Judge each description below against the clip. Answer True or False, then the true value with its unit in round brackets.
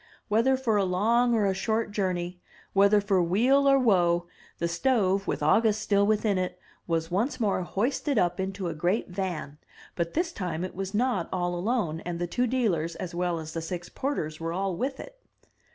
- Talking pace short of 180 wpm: False (195 wpm)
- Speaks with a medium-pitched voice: False (195 Hz)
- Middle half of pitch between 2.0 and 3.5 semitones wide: False (4.6 semitones)